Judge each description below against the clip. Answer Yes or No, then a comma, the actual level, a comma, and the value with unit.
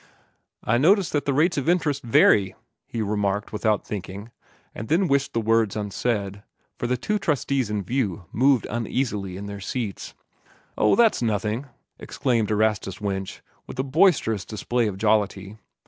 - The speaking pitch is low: Yes, low, 110 Hz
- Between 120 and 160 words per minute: Yes, average, 155 wpm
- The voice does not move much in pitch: No, average, 4.7 semitones